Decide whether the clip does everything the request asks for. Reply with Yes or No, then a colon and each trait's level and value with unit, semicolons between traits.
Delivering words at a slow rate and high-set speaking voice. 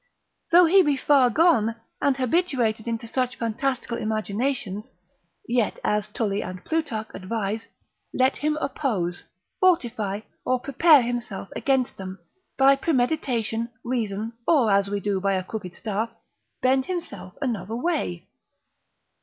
Yes: slow, 130 wpm; high, 235 Hz